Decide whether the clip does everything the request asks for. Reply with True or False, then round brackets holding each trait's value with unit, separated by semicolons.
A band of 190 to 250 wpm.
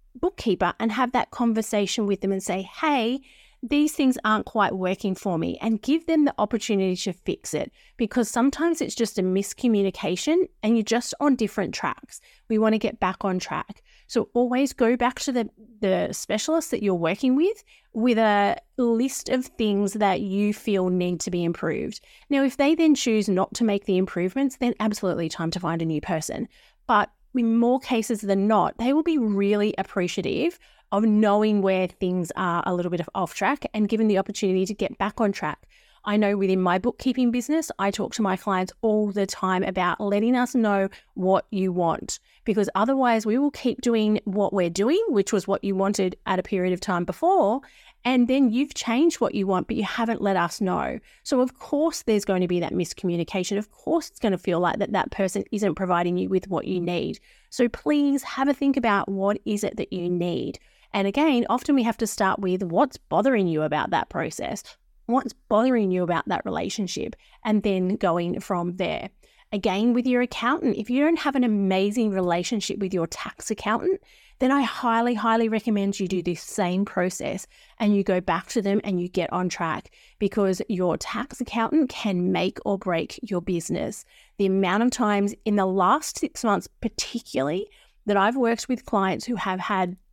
True (200 wpm)